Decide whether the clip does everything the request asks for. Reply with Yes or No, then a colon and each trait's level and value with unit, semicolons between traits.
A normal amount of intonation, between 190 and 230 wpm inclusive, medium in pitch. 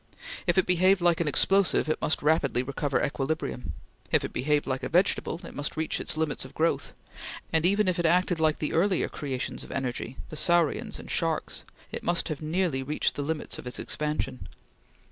Yes: average, 3.3 semitones; average, 195 wpm; medium, 160 Hz